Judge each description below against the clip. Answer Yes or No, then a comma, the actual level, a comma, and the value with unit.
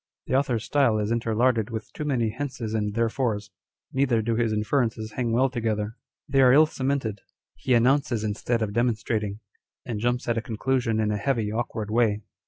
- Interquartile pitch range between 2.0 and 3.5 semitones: Yes, average, 2.9 semitones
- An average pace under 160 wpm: No, average, 180 wpm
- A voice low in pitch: Yes, low, 115 Hz